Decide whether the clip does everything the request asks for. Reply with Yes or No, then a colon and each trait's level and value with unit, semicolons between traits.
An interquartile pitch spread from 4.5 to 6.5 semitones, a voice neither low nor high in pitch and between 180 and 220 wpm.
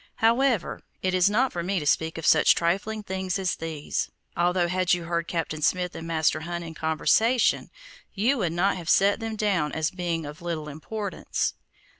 No: average, 3.5 semitones; medium, 175 Hz; average, 185 wpm